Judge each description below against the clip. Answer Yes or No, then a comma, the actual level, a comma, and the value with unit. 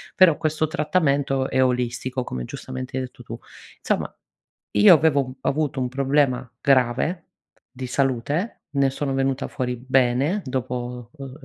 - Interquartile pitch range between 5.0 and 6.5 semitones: No, narrow, 2.5 semitones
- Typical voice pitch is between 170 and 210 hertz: No, low, 135 Hz